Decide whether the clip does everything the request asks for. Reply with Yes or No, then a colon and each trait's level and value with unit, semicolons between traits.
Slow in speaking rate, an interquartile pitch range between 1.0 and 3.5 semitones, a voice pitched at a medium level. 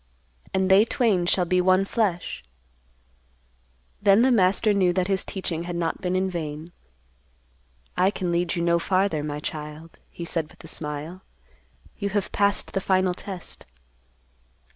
No: average, 155 wpm; narrow, 2.5 semitones; medium, 180 Hz